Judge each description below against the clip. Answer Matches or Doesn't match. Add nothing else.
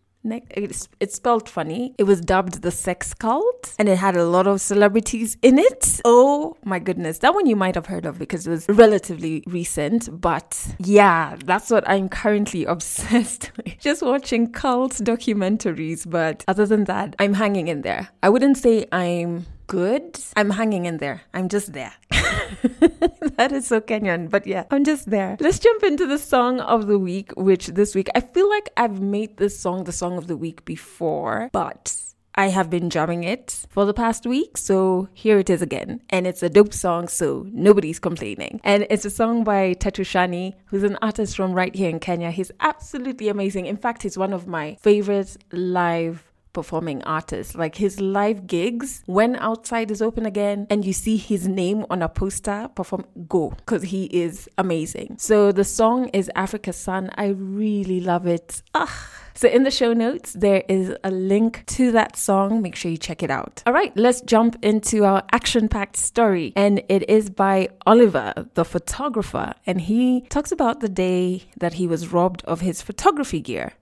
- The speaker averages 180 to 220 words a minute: Matches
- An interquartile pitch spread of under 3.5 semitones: Doesn't match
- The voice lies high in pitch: Matches